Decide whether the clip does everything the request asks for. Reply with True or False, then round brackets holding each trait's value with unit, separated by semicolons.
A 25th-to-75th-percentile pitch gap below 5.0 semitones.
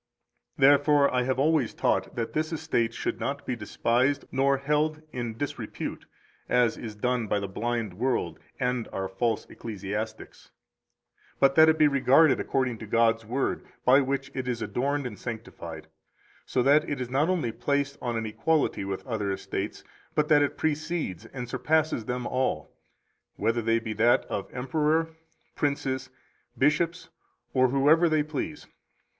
True (4.1 semitones)